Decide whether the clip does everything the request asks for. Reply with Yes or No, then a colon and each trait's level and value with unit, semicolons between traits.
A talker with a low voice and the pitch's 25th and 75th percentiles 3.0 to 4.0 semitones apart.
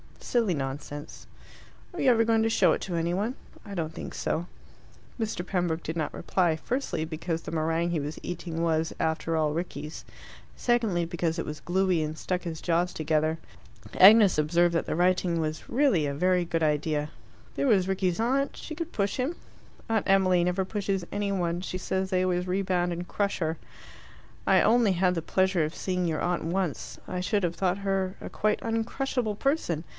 No: medium, 180 Hz; average, 3.4 semitones